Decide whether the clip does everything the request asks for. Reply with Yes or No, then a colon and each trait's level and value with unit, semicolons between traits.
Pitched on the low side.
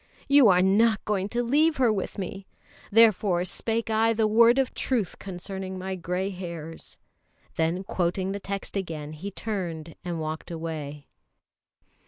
No: high, 190 Hz